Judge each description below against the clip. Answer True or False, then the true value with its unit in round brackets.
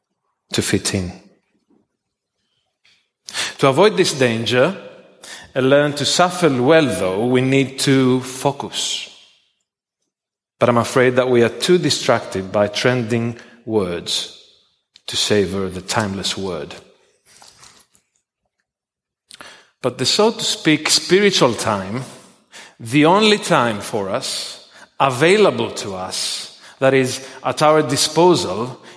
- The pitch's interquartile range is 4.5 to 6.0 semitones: True (4.8 semitones)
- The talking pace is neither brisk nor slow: False (110 wpm)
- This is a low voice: True (130 Hz)